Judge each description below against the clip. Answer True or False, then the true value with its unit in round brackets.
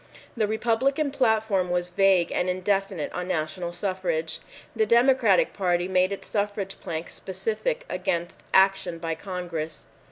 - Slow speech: True (130 wpm)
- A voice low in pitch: False (190 Hz)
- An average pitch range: True (3.5 semitones)